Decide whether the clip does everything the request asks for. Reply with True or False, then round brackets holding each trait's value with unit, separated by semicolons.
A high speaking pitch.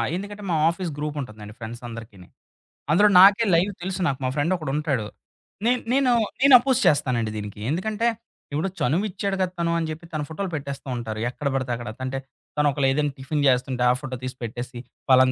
False (145 Hz)